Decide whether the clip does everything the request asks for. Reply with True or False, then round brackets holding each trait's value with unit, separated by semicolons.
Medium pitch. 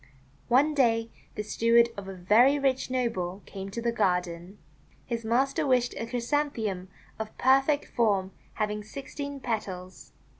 False (230 Hz)